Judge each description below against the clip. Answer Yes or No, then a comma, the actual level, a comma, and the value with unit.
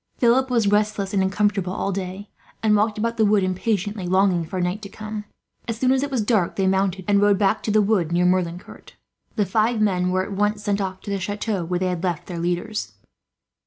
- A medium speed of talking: No, fast, 225 wpm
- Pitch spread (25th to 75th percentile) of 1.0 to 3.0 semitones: Yes, narrow, 2.5 semitones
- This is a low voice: No, high, 200 Hz